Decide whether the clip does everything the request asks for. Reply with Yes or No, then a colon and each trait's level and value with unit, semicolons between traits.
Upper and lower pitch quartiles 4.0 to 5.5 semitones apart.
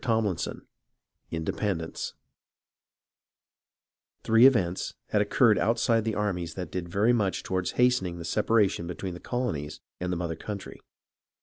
Yes: average, 4.6 semitones